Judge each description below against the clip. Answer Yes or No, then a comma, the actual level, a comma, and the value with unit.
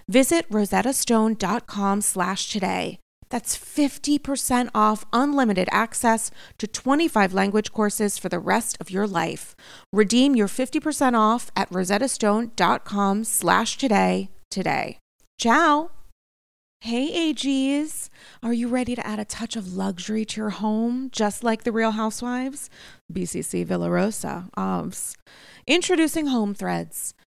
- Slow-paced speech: Yes, slow, 110 wpm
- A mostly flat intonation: No, average, 4.2 semitones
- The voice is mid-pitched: No, high, 220 Hz